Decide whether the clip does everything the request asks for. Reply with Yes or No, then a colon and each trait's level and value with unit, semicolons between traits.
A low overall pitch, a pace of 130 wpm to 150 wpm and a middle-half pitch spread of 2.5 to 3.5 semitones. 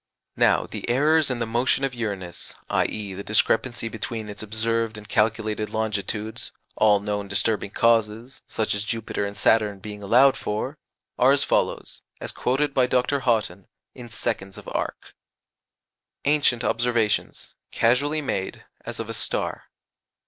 Yes: low, 110 Hz; average, 145 wpm; average, 3.1 semitones